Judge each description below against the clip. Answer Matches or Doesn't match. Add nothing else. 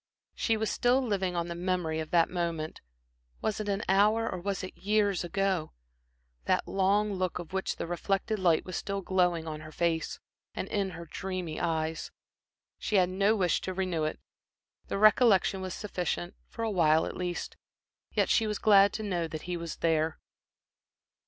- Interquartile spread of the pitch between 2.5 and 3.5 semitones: Matches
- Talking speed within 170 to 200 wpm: Matches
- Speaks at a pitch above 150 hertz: Matches